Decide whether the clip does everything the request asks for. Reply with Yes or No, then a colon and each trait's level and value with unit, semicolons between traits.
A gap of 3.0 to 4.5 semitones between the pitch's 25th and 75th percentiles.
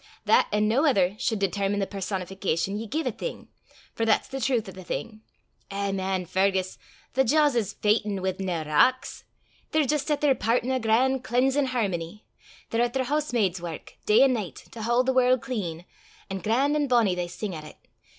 No: average, 5.2 semitones